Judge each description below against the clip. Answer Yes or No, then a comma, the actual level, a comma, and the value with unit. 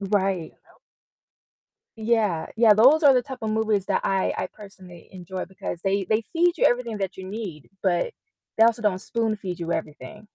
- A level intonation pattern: No, average, 3.3 semitones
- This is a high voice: Yes, high, 205 Hz